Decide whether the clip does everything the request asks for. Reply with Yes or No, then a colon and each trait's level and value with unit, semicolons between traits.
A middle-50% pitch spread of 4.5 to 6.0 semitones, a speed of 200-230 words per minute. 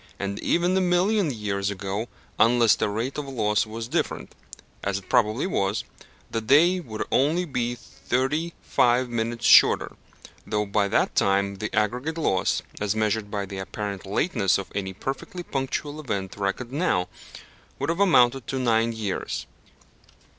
No: wide, 5.4 semitones; average, 155 wpm